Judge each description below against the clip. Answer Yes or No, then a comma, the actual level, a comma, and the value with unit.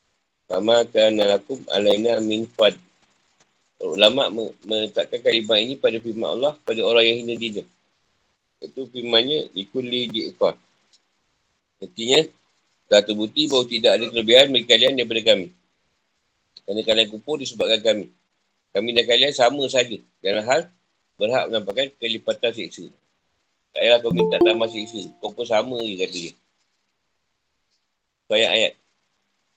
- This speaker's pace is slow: No, average, 120 wpm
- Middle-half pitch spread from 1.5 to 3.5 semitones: Yes, average, 3.0 semitones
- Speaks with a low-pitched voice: Yes, low, 115 Hz